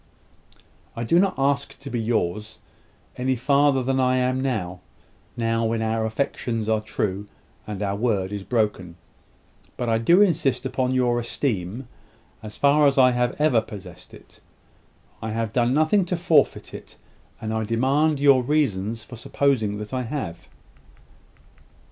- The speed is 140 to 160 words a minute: Yes, average, 155 wpm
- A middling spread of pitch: Yes, average, 3.8 semitones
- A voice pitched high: No, low, 120 Hz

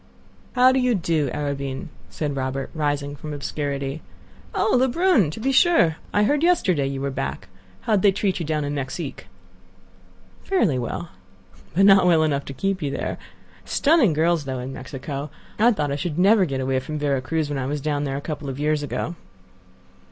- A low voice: No, medium, 150 Hz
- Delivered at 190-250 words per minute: Yes, average, 195 wpm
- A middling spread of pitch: No, wide, 5.7 semitones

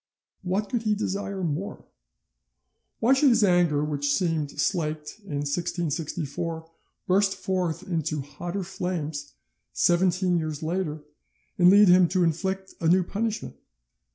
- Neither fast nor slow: No, slow, 125 wpm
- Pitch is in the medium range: Yes, medium, 175 Hz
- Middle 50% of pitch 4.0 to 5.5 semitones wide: No, average, 3.4 semitones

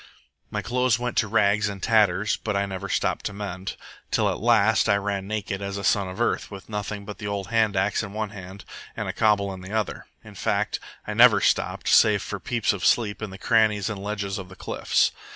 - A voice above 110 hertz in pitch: No, low, 100 Hz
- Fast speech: Yes, fast, 225 wpm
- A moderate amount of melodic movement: No, narrow, 1.7 semitones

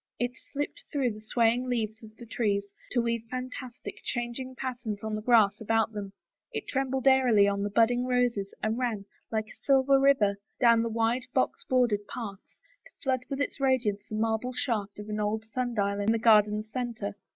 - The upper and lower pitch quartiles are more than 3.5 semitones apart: No, average, 3.0 semitones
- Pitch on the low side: No, high, 230 Hz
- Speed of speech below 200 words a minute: Yes, average, 190 wpm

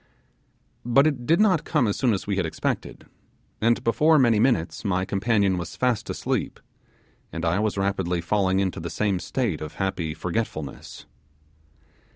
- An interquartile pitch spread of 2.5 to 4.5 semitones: No, average, 4.9 semitones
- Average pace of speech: Yes, average, 160 wpm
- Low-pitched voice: Yes, low, 100 Hz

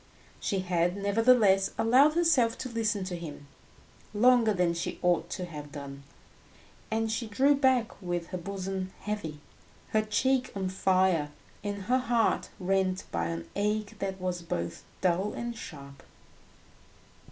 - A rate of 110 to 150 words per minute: Yes, average, 140 wpm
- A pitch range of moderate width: Yes, average, 4.3 semitones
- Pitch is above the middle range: Yes, high, 195 Hz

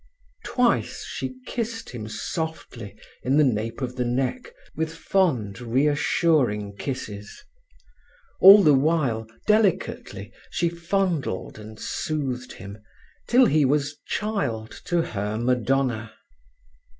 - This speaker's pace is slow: Yes, slow, 110 wpm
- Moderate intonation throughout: No, wide, 7.1 semitones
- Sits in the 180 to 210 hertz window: No, low, 135 Hz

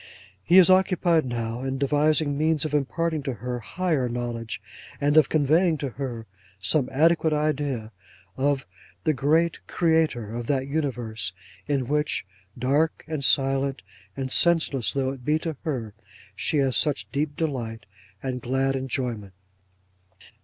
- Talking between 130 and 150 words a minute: Yes, average, 140 wpm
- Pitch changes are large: No, average, 3.9 semitones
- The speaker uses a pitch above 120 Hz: Yes, medium, 140 Hz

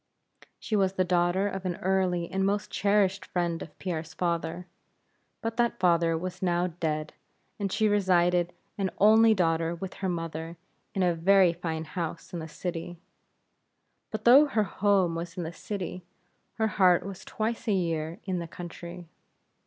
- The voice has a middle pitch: Yes, medium, 180 Hz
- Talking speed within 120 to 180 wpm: Yes, average, 165 wpm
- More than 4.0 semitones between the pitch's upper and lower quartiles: No, narrow, 2.5 semitones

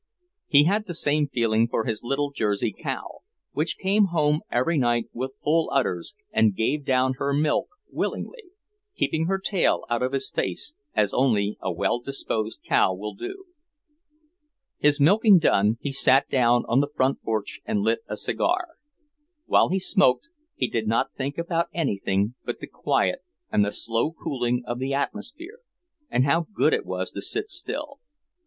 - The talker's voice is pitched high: No, low, 135 Hz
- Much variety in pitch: Yes, wide, 6.3 semitones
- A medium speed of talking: Yes, average, 170 wpm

